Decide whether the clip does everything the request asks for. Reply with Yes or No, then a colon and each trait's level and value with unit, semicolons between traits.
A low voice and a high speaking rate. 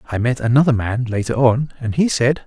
Yes: low, 125 Hz; fast, 220 wpm